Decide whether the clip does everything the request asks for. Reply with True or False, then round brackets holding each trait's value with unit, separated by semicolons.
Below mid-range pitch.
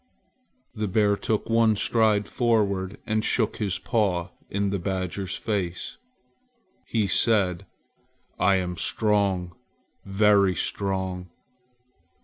True (100 Hz)